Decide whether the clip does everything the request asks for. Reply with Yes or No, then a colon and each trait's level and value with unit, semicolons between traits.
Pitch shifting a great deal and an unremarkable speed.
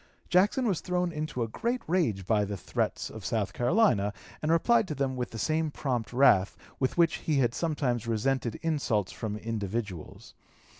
Yes: wide, 6.9 semitones; average, 170 wpm